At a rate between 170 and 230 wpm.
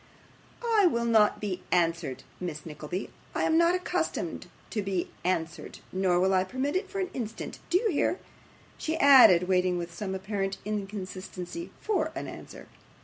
No: average, 160 wpm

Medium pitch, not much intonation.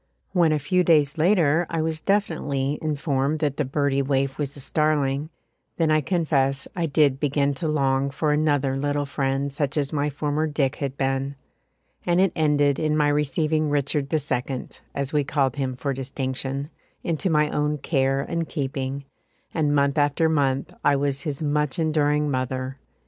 Yes: medium, 145 Hz; narrow, 2.1 semitones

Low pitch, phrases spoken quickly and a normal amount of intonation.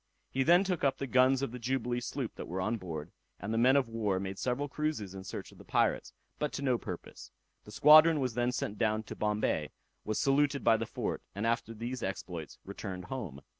Yes: low, 115 Hz; fast, 220 wpm; average, 4.8 semitones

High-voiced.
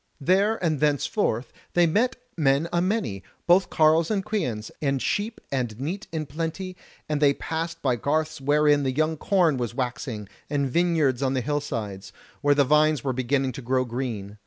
No: medium, 145 Hz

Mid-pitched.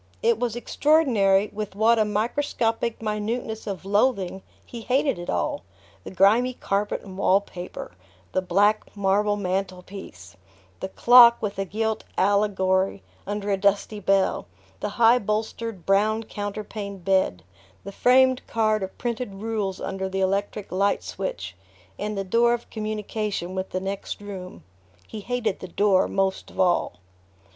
No: high, 205 Hz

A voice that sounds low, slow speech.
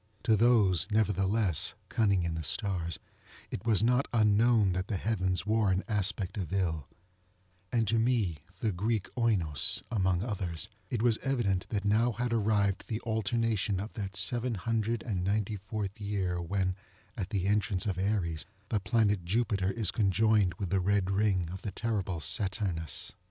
No: low, 100 Hz; average, 160 wpm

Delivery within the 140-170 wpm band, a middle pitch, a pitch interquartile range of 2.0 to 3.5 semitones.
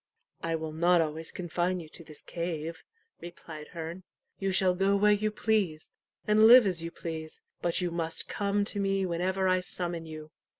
No: average, 180 wpm; medium, 175 Hz; average, 3.0 semitones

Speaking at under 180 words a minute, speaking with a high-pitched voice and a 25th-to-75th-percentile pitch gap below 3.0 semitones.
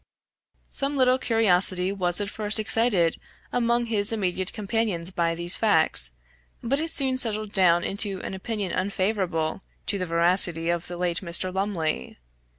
No: average, 150 wpm; high, 195 Hz; average, 4.2 semitones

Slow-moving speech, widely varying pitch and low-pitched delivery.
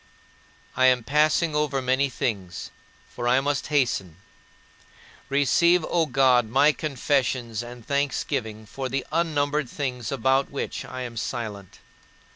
No: slow, 130 wpm; average, 3.0 semitones; low, 130 Hz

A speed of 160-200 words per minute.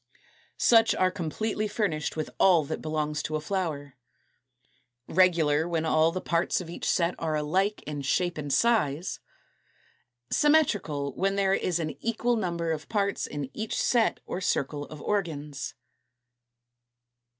No: average, 140 wpm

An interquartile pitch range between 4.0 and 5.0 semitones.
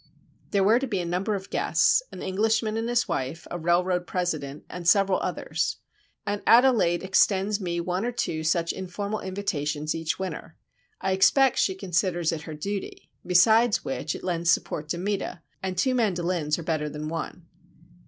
No: average, 3.3 semitones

